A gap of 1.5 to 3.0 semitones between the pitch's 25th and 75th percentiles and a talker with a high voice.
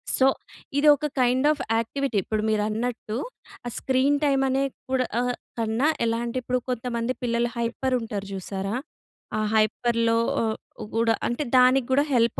Yes: narrow, 2.4 semitones; high, 240 Hz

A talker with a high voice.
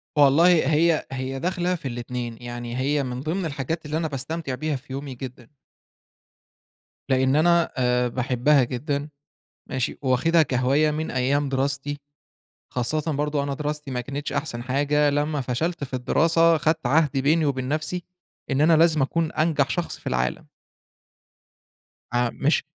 No: medium, 145 Hz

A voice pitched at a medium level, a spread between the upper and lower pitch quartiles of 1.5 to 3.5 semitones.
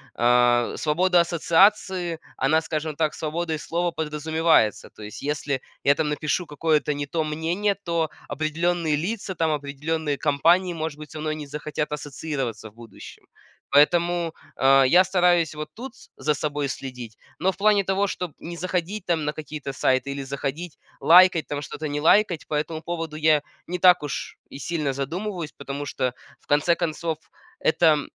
Yes: medium, 155 Hz; average, 2.9 semitones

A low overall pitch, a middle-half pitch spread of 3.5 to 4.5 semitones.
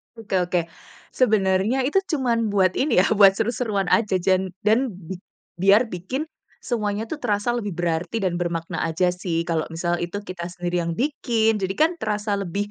No: high, 200 Hz; average, 4.0 semitones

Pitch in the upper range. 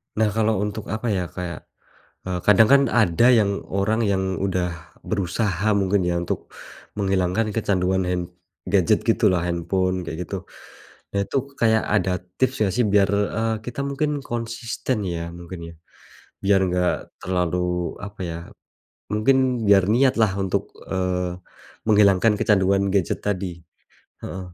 No: low, 100 Hz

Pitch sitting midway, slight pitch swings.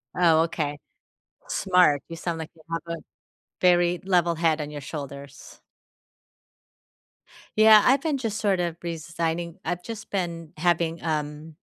Yes: medium, 170 Hz; narrow, 2.1 semitones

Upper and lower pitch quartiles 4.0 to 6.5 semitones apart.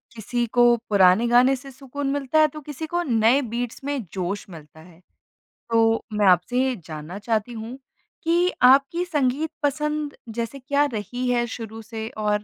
Yes: average, 4.5 semitones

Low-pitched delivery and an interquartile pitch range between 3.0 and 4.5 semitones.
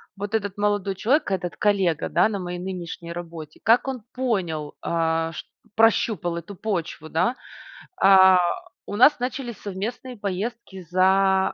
No: high, 195 Hz; average, 4.0 semitones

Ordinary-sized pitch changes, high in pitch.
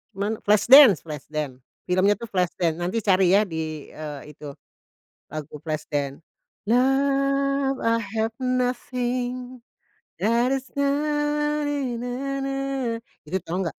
No: wide, 6.6 semitones; high, 240 Hz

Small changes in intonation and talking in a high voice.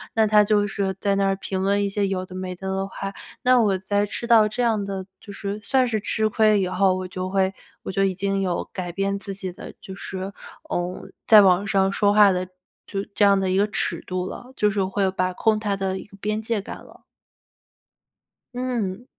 Yes: narrow, 1.8 semitones; high, 195 Hz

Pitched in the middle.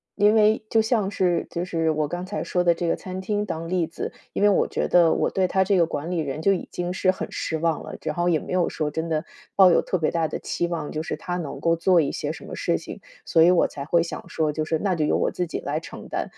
Yes: medium, 175 Hz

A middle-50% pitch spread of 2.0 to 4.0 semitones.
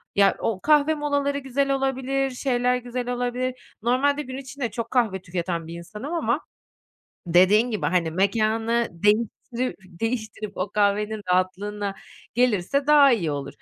No: average, 4.9 semitones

